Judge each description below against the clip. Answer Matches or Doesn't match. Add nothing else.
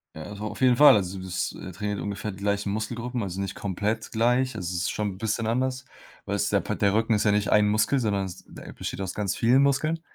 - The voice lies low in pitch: Matches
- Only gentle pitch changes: Doesn't match